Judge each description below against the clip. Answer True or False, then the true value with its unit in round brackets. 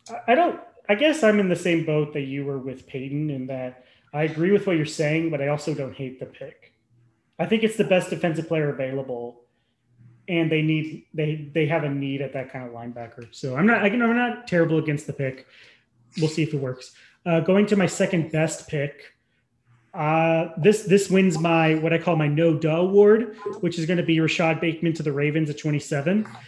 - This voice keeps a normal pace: False (215 wpm)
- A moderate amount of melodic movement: True (4.6 semitones)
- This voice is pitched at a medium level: True (155 Hz)